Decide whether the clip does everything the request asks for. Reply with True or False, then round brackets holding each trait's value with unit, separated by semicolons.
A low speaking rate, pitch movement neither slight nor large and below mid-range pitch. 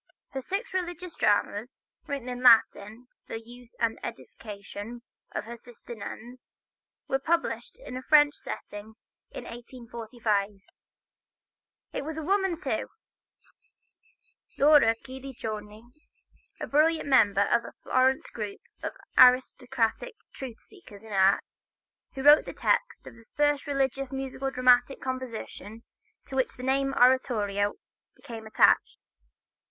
False (125 wpm; 3.5 semitones; 250 Hz)